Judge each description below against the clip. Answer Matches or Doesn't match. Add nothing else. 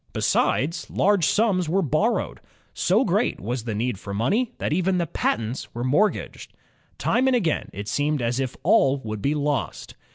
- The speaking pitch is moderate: Matches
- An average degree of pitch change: Doesn't match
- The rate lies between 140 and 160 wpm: Doesn't match